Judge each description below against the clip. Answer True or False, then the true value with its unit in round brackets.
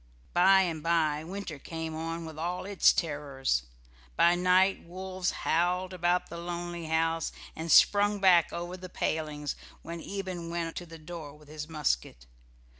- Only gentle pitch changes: True (2.3 semitones)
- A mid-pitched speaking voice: True (170 Hz)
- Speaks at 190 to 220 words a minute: False (155 wpm)